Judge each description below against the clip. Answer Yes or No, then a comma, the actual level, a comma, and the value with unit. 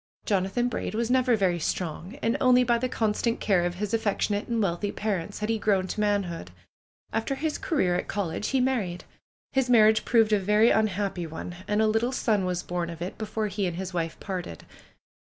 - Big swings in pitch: No, average, 3.8 semitones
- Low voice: No, high, 210 Hz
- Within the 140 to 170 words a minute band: No, fast, 205 wpm